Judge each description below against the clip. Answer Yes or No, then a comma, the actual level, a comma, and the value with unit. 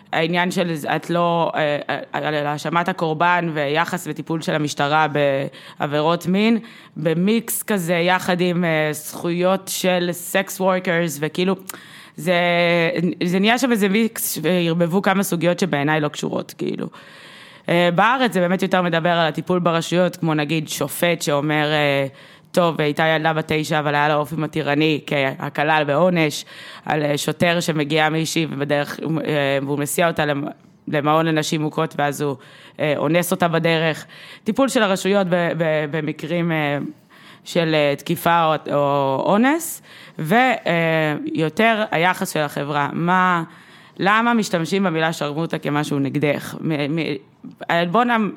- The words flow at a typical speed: Yes, average, 120 wpm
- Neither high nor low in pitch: Yes, medium, 165 Hz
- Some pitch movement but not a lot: Yes, average, 3.1 semitones